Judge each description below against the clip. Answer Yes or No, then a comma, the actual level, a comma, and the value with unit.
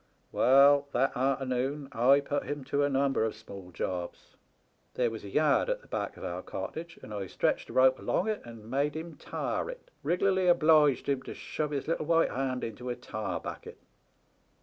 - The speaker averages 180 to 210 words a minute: Yes, average, 195 wpm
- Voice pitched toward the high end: No, low, 135 Hz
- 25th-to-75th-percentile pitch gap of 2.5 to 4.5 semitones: Yes, average, 4.0 semitones